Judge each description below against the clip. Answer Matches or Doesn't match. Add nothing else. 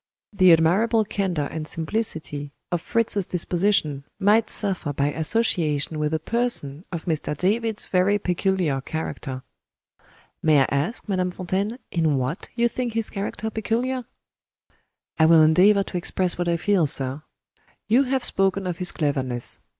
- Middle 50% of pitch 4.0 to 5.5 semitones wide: Matches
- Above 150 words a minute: Doesn't match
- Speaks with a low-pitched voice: Doesn't match